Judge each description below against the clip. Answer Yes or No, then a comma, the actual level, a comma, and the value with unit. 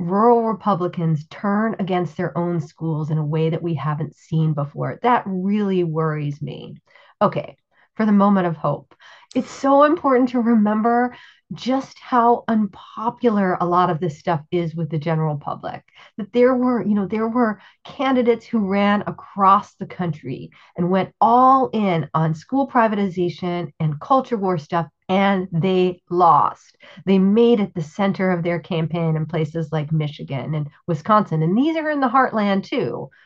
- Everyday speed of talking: Yes, average, 165 wpm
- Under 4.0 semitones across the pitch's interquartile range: No, wide, 5.5 semitones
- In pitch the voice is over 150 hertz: Yes, medium, 185 Hz